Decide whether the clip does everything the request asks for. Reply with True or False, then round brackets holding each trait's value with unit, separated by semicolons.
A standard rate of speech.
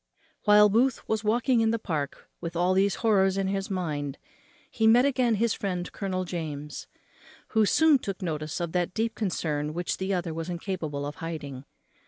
True (180 wpm)